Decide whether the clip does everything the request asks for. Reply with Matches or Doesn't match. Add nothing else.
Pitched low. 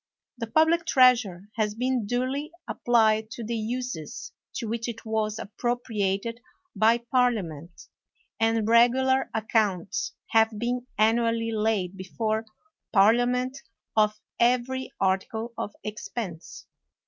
Doesn't match